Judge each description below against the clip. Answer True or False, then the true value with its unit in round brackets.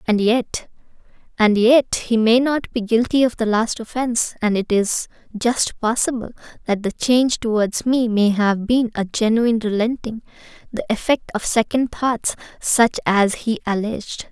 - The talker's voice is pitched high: True (225 Hz)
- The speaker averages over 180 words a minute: False (150 wpm)